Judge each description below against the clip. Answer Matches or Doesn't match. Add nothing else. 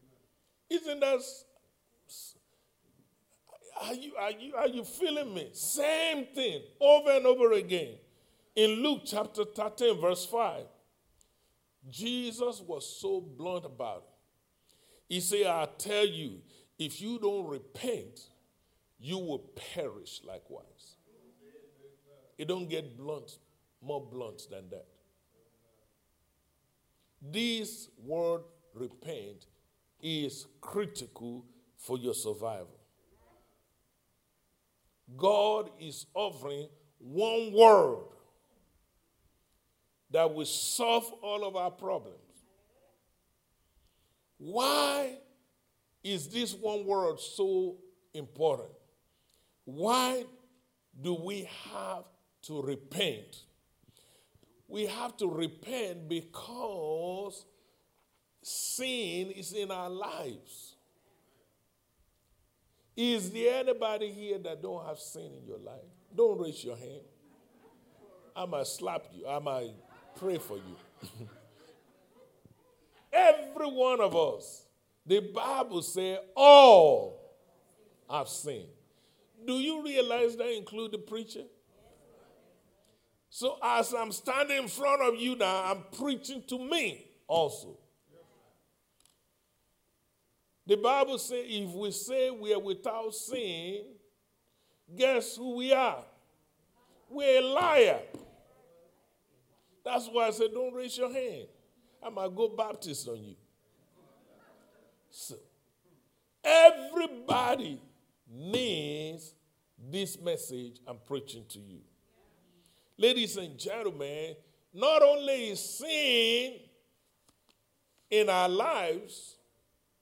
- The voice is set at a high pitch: Matches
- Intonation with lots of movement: Matches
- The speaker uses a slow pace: Matches